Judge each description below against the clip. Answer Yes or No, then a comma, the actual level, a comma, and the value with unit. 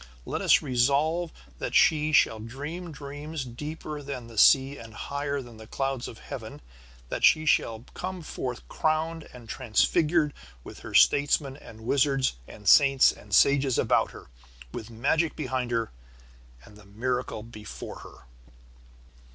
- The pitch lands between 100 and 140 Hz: Yes, low, 135 Hz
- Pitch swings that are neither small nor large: Yes, average, 4.3 semitones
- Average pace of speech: Yes, average, 145 wpm